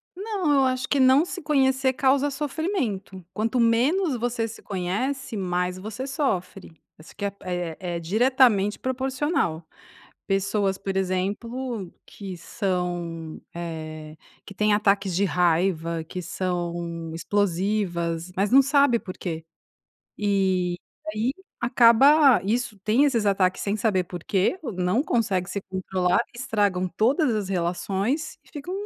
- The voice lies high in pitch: Yes, high, 200 Hz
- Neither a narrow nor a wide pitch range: No, wide, 6.1 semitones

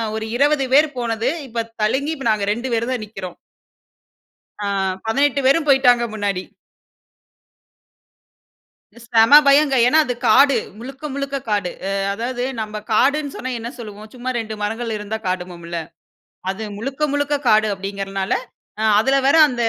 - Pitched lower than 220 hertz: No, high, 235 Hz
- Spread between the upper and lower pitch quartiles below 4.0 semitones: No, average, 4.3 semitones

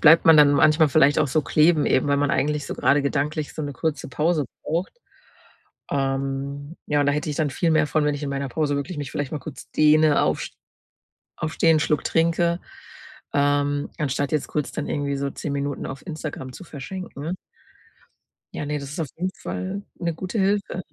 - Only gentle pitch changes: Yes, narrow, 2.1 semitones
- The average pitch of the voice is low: No, medium, 150 Hz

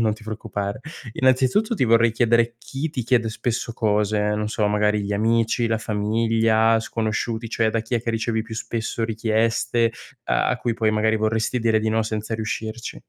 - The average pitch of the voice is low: Yes, low, 110 Hz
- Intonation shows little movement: Yes, narrow, 1.2 semitones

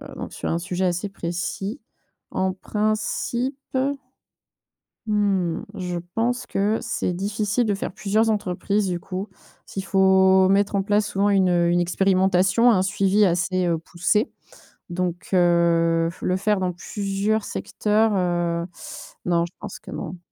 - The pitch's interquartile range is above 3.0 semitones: No, average, 2.7 semitones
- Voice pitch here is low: No, high, 190 Hz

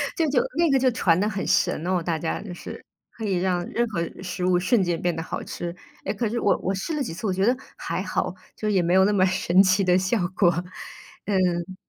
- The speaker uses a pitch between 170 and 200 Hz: Yes, medium, 185 Hz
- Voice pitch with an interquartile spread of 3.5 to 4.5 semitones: No, average, 3.0 semitones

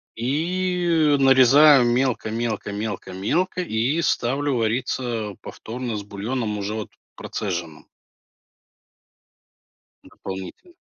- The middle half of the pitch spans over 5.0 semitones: Yes, wide, 5.4 semitones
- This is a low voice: Yes, low, 120 Hz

